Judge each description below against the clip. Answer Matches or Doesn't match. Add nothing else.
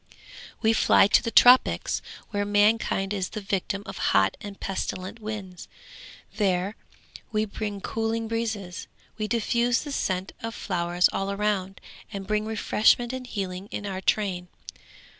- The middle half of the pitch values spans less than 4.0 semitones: Matches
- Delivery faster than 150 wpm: Doesn't match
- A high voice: Matches